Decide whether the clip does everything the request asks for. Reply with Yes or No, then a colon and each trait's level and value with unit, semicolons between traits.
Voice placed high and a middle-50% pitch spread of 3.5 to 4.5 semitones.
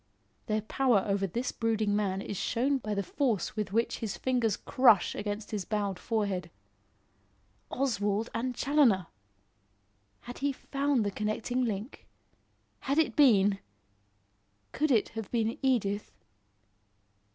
Yes: high, 220 Hz; average, 3.8 semitones